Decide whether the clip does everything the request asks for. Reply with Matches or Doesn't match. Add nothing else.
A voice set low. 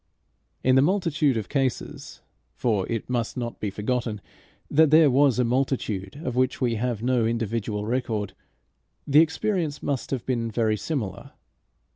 Matches